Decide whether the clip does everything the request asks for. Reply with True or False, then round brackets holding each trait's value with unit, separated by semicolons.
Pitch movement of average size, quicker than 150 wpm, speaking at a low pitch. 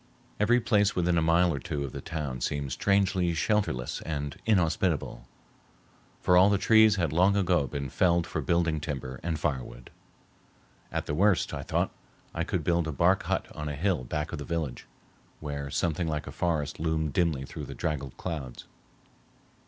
True (3.9 semitones; 175 wpm; 80 Hz)